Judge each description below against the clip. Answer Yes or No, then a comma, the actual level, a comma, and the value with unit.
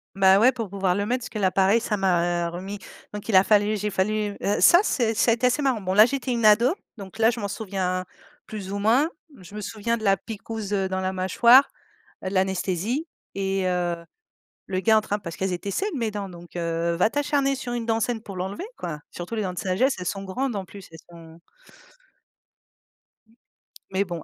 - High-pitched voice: Yes, high, 200 Hz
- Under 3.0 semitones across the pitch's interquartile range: No, average, 3.3 semitones